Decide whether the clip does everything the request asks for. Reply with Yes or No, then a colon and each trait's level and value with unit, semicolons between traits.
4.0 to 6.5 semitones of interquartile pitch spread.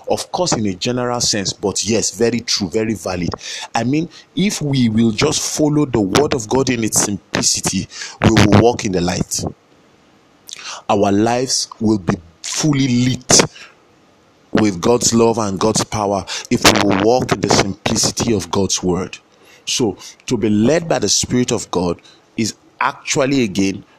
No: average, 3.5 semitones